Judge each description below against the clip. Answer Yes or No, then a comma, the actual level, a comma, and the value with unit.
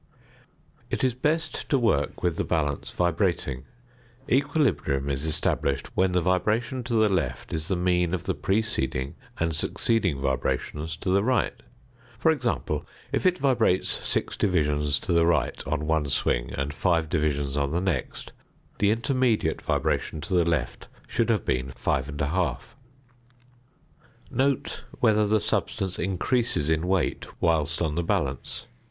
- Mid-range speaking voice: No, very low, 85 Hz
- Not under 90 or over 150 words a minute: Yes, average, 145 wpm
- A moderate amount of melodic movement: No, wide, 6.4 semitones